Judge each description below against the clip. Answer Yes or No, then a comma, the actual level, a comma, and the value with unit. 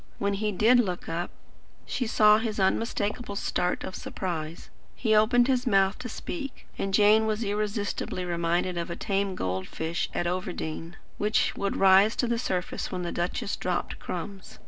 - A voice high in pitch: Yes, high, 195 Hz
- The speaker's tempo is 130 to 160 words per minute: No, average, 170 wpm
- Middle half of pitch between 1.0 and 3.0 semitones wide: No, average, 3.4 semitones